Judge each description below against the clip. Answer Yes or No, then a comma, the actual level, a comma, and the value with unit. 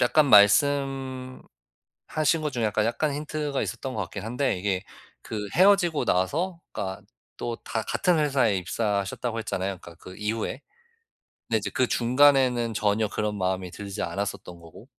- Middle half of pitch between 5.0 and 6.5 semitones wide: Yes, wide, 5.6 semitones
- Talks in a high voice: No, low, 115 Hz